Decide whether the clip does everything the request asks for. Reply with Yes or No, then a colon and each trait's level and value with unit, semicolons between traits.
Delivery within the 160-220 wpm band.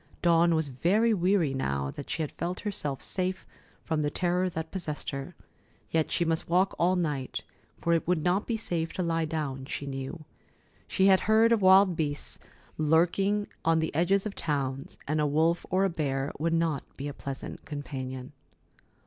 Yes: average, 180 wpm